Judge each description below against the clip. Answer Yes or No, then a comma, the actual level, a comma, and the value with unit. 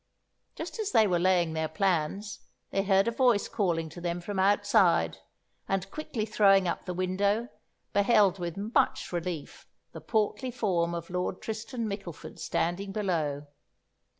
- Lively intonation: No, average, 3.4 semitones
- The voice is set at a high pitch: Yes, high, 195 Hz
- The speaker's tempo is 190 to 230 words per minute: No, average, 150 wpm